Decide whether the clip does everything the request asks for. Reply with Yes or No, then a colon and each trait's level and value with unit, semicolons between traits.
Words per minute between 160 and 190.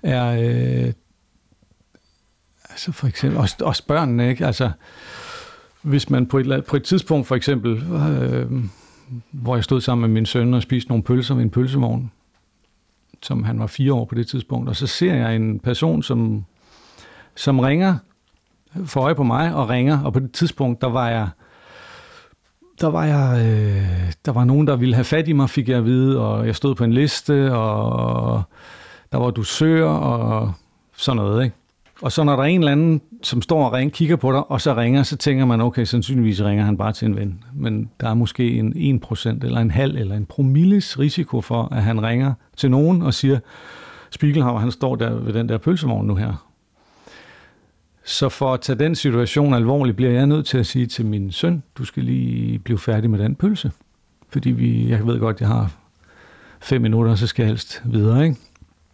No: average, 200 wpm